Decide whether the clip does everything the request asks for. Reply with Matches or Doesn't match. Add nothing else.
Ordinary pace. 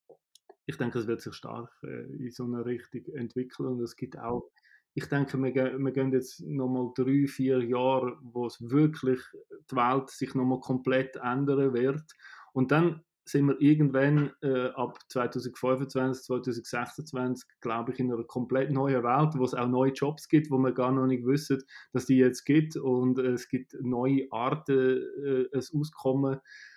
Matches